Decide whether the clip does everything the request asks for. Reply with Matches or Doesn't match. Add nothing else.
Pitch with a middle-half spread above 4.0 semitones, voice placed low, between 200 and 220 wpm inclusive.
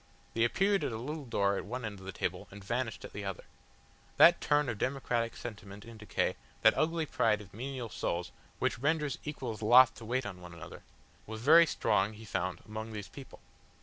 Matches